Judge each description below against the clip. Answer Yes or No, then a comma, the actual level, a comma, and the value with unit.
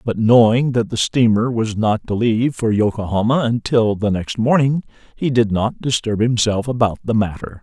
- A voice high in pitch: No, low, 115 Hz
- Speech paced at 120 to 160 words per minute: No, average, 180 wpm